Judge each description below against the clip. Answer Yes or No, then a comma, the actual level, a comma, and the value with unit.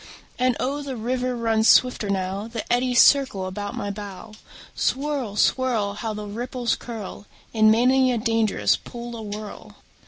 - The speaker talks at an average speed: Yes, average, 150 wpm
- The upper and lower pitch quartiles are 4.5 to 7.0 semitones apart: No, average, 3.3 semitones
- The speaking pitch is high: Yes, high, 230 Hz